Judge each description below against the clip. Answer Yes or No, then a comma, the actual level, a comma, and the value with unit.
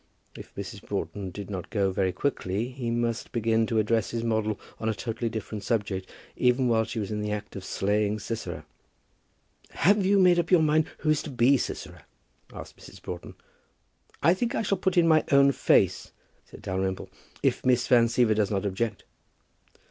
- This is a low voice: Yes, low, 115 Hz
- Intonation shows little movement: No, average, 4.8 semitones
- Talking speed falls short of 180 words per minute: No, average, 185 wpm